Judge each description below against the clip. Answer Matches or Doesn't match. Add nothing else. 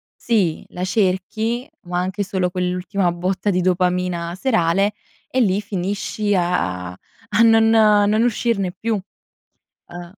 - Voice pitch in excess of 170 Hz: Matches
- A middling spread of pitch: Matches